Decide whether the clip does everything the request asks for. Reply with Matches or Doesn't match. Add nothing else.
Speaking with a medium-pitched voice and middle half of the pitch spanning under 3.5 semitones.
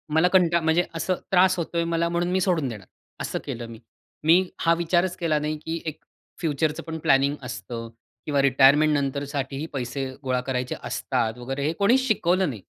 Doesn't match